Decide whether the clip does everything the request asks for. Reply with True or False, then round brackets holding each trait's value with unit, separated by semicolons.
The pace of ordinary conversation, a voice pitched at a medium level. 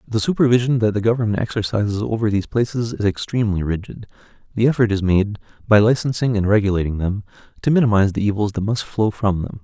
False (185 wpm; 105 Hz)